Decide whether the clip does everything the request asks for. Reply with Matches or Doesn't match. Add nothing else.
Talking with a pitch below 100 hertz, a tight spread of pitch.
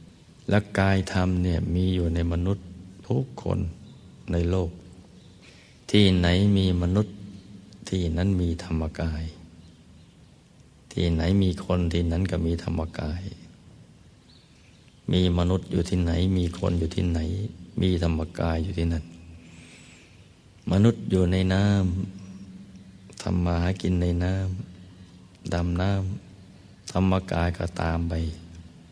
Matches